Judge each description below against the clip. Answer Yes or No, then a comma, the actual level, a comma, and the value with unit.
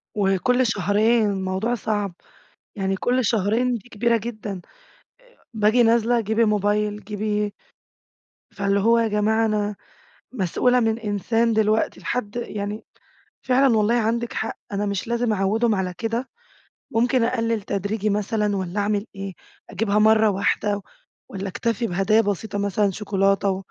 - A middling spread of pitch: No, narrow, 2.3 semitones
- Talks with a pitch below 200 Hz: No, high, 210 Hz